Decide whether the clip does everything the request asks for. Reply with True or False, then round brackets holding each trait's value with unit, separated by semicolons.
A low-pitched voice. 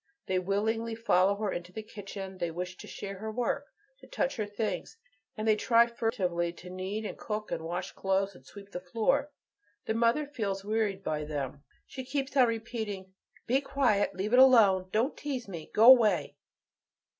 False (210 Hz)